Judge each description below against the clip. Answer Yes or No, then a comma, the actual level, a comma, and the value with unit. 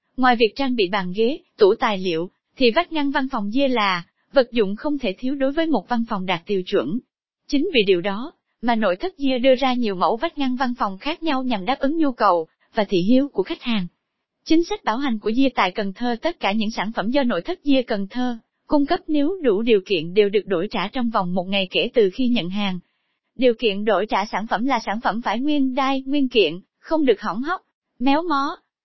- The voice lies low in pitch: No, high, 245 Hz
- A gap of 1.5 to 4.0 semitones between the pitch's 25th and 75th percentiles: No, average, 5.0 semitones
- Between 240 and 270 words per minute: Yes, average, 245 wpm